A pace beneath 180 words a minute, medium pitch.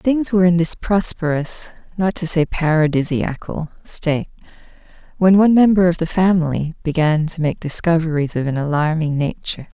Yes: average, 145 wpm; medium, 165 Hz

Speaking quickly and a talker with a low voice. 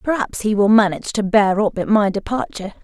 No: fast, 210 wpm; high, 210 Hz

